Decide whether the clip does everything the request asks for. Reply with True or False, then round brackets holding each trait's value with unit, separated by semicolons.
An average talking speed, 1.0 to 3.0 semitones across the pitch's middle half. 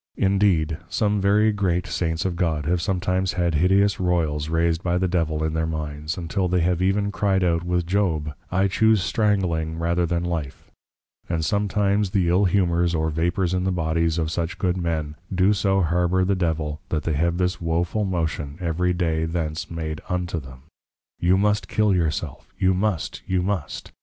True (180 wpm; 2.7 semitones)